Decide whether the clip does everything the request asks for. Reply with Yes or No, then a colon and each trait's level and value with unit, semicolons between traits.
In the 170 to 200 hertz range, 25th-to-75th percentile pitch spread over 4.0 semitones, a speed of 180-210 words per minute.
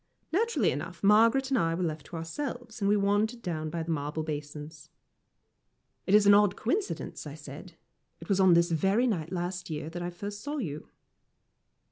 Yes: medium, 185 Hz; average, 5.1 semitones; average, 185 wpm